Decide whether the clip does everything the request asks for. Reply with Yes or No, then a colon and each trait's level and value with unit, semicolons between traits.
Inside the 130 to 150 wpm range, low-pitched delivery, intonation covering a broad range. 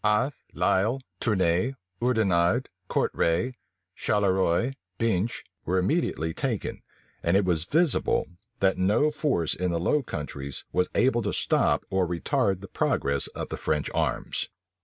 Yes: slow, 135 wpm; very low, 95 Hz; wide, 5.9 semitones